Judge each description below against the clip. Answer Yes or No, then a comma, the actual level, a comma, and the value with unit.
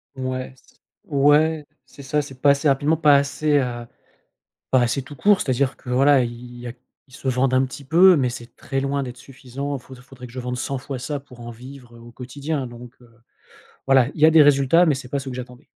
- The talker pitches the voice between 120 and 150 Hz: Yes, low, 135 Hz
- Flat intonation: Yes, narrow, 2.3 semitones